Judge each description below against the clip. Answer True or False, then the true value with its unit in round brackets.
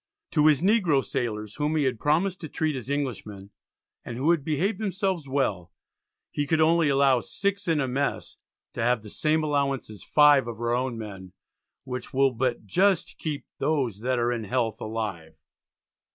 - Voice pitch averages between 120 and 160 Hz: True (135 Hz)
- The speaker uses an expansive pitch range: False (4.9 semitones)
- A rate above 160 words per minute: True (180 wpm)